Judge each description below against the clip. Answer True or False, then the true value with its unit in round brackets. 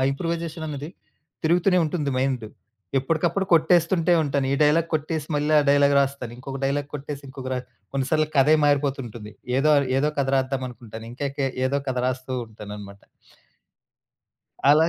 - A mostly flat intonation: False (3.0 semitones)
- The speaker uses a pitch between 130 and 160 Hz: True (140 Hz)